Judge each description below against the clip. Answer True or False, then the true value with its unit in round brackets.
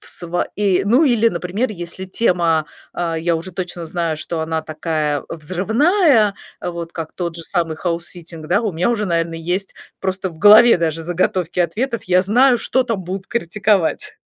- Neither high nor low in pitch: True (180 Hz)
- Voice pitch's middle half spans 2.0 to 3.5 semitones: False (3.9 semitones)